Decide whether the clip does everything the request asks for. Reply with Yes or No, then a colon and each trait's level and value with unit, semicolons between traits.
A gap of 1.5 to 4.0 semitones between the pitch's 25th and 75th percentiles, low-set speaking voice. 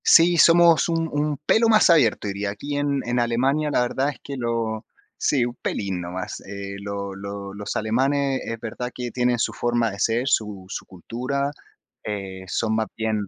No: wide, 5.5 semitones; low, 120 Hz